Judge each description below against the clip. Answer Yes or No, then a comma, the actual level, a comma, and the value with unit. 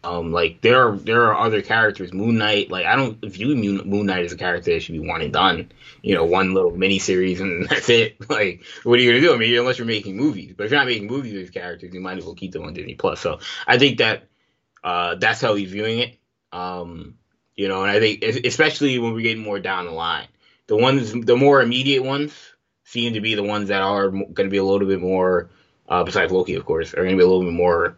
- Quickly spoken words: Yes, fast, 255 wpm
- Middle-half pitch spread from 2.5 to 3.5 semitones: No, average, 4.3 semitones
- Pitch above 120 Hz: No, low, 105 Hz